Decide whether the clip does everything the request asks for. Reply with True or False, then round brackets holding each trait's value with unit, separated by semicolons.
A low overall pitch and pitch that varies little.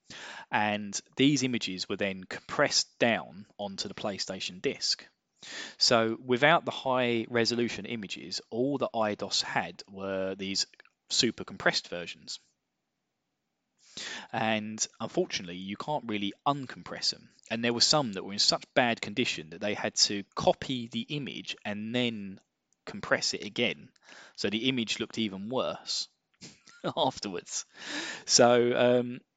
False (115 Hz; 3.3 semitones)